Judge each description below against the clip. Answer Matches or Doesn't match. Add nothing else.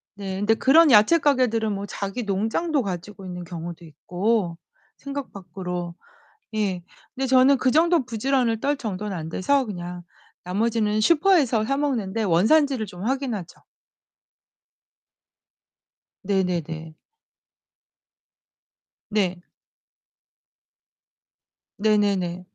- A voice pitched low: Doesn't match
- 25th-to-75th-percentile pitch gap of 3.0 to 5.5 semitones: Doesn't match